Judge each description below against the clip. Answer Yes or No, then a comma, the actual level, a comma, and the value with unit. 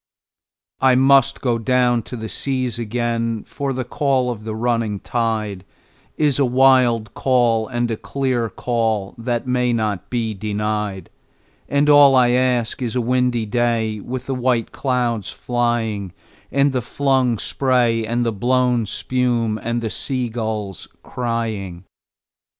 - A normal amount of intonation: No, narrow, 2.3 semitones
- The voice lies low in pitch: Yes, low, 120 Hz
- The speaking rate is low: No, average, 145 wpm